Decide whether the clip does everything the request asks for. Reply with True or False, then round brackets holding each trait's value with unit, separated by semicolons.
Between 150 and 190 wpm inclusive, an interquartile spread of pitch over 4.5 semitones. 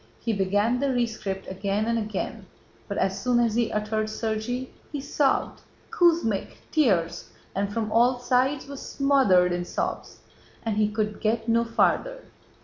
False (160 wpm; 3.2 semitones)